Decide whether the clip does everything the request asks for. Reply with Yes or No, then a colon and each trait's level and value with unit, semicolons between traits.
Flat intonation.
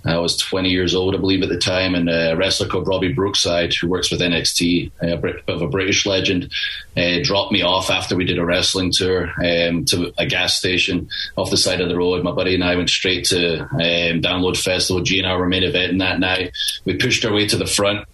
Yes: narrow, 1.4 semitones